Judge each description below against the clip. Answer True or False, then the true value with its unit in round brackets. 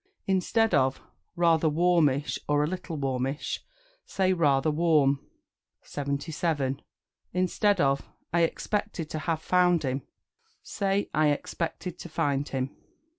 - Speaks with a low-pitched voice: False (160 Hz)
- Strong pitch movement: False (4.0 semitones)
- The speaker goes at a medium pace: False (120 wpm)